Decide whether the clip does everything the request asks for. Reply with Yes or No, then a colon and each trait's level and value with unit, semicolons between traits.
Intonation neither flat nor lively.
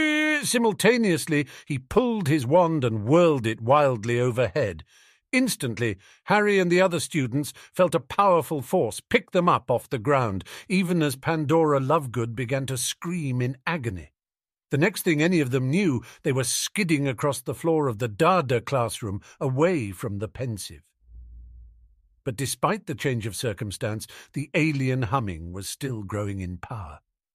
No: wide, 6.5 semitones